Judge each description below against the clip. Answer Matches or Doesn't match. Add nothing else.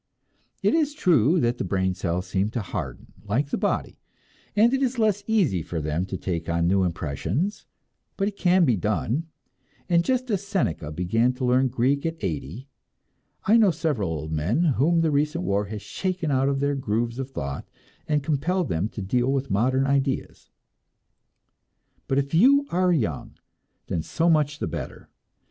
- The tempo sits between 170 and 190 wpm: Matches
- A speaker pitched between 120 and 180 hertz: Matches